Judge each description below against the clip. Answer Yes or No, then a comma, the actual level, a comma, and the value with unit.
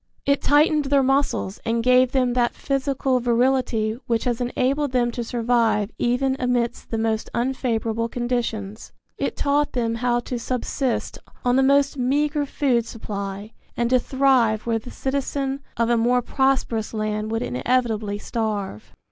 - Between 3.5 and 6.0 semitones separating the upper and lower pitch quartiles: No, average, 2.8 semitones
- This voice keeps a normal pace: Yes, average, 150 wpm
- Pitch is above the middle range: Yes, high, 245 Hz